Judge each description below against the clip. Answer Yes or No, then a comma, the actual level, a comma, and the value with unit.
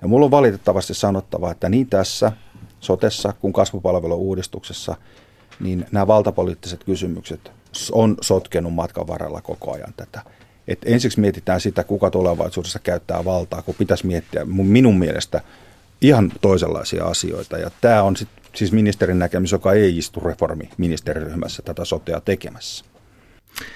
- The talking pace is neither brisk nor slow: Yes, average, 130 wpm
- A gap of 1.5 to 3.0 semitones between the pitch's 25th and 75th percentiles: Yes, average, 2.7 semitones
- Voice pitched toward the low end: Yes, very low, 95 Hz